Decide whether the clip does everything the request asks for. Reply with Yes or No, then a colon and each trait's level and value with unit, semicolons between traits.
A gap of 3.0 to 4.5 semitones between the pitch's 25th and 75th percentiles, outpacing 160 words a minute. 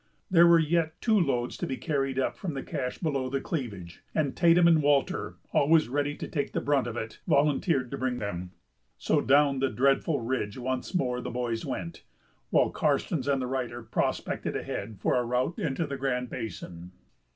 Yes: average, 3.3 semitones; average, 190 wpm